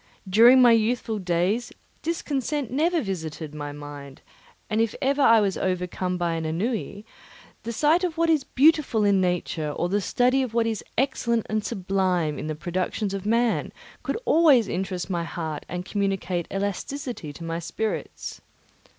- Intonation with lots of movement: Yes, wide, 5.7 semitones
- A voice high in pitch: Yes, high, 200 Hz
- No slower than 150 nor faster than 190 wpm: Yes, average, 160 wpm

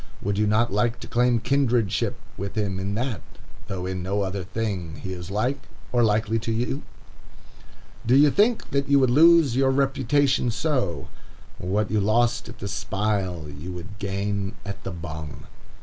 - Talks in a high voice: No, low, 110 Hz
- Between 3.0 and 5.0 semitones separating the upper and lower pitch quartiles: Yes, average, 4.4 semitones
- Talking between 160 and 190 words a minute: Yes, average, 170 wpm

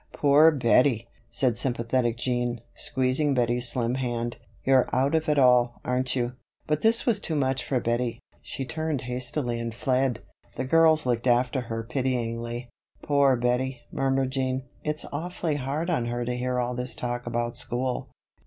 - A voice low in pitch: Yes, low, 125 Hz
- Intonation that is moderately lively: No, narrow, 2.2 semitones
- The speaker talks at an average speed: Yes, average, 165 wpm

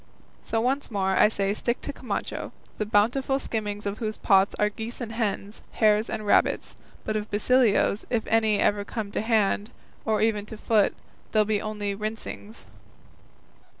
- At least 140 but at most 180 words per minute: Yes, average, 170 wpm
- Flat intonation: Yes, narrow, 1.6 semitones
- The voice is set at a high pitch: Yes, high, 215 Hz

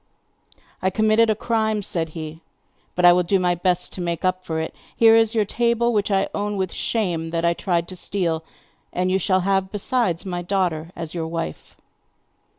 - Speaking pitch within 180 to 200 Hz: Yes, medium, 185 Hz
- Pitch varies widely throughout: No, average, 3.5 semitones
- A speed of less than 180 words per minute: No, average, 195 wpm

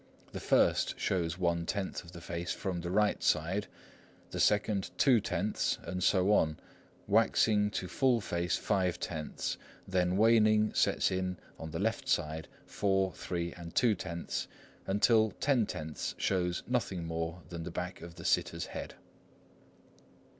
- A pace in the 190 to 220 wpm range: No, average, 150 wpm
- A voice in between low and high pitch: No, very low, 90 Hz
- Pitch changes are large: No, average, 3.5 semitones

